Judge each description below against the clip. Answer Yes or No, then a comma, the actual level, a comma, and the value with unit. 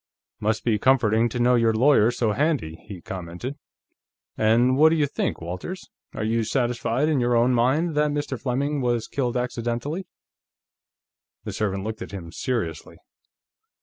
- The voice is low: Yes, low, 120 Hz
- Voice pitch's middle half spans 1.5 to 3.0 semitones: No, average, 4.0 semitones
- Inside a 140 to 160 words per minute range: Yes, average, 155 wpm